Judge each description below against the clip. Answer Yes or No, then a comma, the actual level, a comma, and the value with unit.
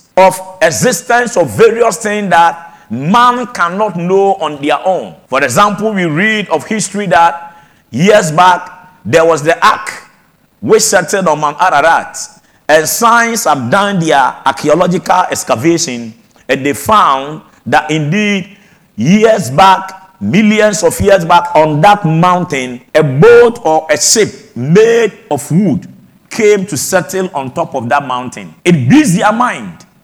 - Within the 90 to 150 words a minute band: Yes, average, 140 wpm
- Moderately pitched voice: Yes, medium, 180 Hz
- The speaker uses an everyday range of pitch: Yes, average, 4.9 semitones